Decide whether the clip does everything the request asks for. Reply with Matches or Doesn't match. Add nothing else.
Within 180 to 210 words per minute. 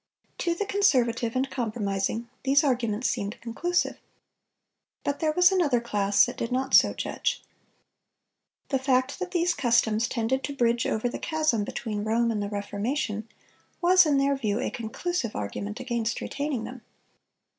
Doesn't match